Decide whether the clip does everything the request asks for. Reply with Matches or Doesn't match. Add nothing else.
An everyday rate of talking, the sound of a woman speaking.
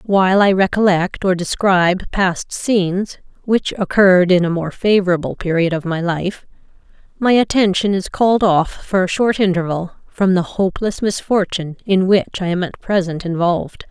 Matches